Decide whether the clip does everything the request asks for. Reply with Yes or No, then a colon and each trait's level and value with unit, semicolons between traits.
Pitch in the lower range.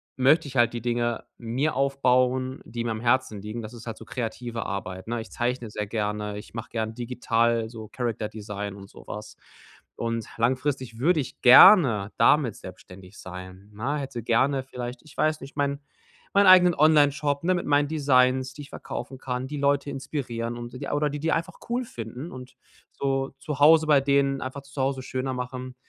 Yes: low, 125 Hz